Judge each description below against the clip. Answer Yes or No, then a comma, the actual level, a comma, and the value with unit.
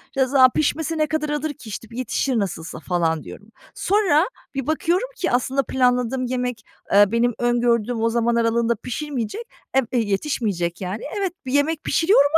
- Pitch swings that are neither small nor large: Yes, average, 4.5 semitones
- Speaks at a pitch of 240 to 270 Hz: Yes, very high, 250 Hz